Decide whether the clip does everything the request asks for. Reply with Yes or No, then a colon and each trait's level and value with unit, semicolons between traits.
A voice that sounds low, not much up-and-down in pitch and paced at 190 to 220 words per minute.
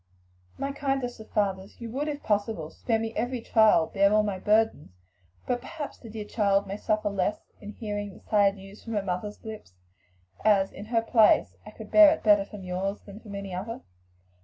No: high, 210 Hz; narrow, 2.3 semitones; average, 200 wpm